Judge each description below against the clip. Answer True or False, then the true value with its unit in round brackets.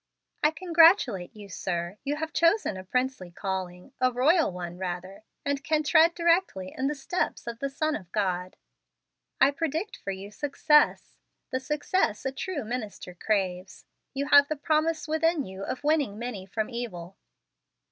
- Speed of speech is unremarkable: True (160 wpm)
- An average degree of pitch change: False (8.3 semitones)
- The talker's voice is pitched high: True (255 Hz)